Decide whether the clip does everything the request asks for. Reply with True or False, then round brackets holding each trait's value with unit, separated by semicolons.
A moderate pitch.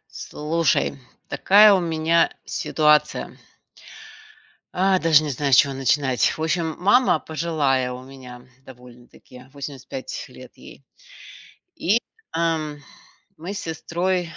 True (155 Hz)